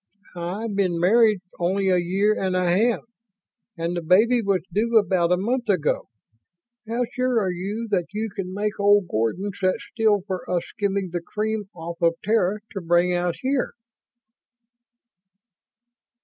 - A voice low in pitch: No, high, 195 Hz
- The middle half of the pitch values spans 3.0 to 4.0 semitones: Yes, average, 3.3 semitones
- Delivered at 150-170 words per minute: Yes, average, 155 wpm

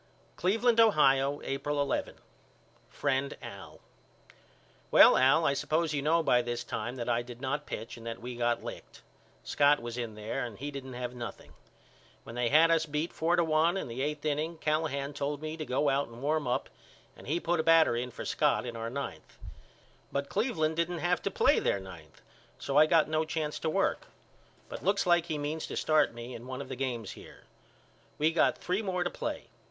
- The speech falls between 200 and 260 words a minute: Yes, fast, 205 wpm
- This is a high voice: No, medium, 145 Hz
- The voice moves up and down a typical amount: Yes, average, 4.5 semitones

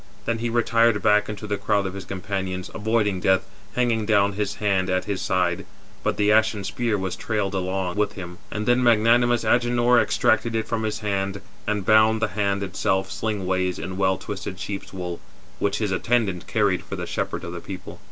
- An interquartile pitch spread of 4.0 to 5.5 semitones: No, average, 2.7 semitones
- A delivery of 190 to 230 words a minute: Yes, average, 195 wpm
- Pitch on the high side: No, low, 100 Hz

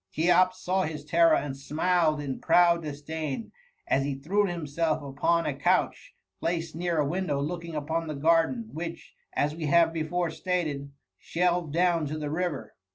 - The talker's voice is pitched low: No, medium, 160 Hz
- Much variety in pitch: No, average, 2.8 semitones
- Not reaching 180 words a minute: Yes, average, 160 wpm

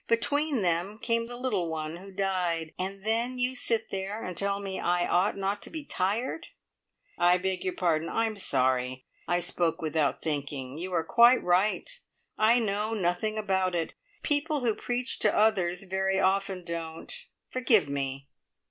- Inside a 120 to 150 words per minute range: No, average, 165 wpm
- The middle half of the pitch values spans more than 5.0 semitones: No, average, 4.3 semitones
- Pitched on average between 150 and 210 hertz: Yes, high, 190 Hz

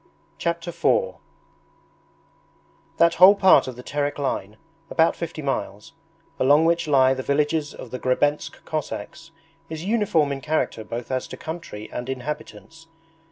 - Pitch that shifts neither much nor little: Yes, average, 4.2 semitones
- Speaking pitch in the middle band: Yes, medium, 145 Hz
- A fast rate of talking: No, average, 140 wpm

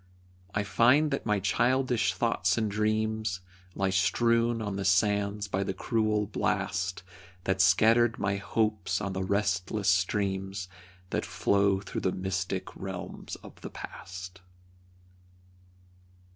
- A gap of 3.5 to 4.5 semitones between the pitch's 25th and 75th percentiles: No, narrow, 2.4 semitones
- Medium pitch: No, low, 100 Hz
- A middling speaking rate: No, slow, 125 wpm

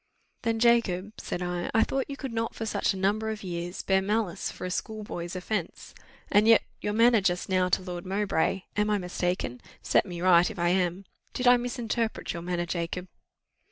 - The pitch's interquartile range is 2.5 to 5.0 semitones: Yes, average, 3.7 semitones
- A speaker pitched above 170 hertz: Yes, high, 190 Hz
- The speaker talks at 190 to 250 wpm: Yes, average, 195 wpm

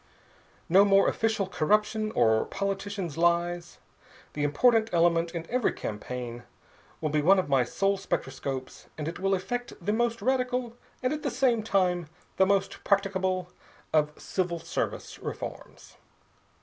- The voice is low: No, high, 190 Hz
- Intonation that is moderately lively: Yes, average, 4.6 semitones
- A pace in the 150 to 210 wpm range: No, average, 140 wpm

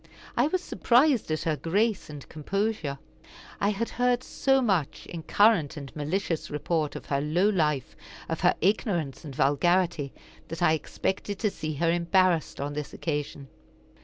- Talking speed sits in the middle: Yes, average, 160 wpm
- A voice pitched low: No, medium, 170 Hz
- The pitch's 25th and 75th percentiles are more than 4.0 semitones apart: Yes, wide, 5.4 semitones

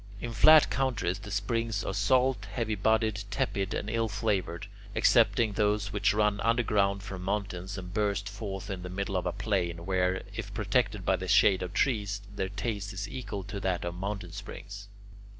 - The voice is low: Yes, low, 100 Hz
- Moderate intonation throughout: No, narrow, 2.2 semitones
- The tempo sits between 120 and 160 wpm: No, average, 180 wpm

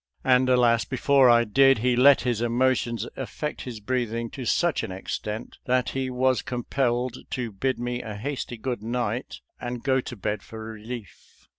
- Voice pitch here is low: Yes, low, 125 Hz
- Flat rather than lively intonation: Yes, narrow, 2.0 semitones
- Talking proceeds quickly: No, average, 175 wpm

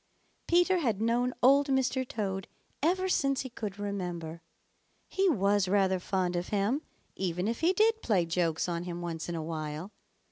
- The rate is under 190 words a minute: Yes, average, 170 wpm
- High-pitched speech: Yes, high, 200 Hz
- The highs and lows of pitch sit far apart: Yes, wide, 7.1 semitones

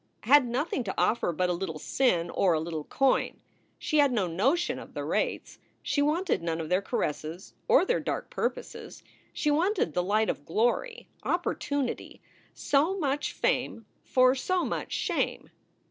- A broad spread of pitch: Yes, wide, 8.7 semitones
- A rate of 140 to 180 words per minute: Yes, average, 160 wpm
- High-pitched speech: Yes, high, 245 Hz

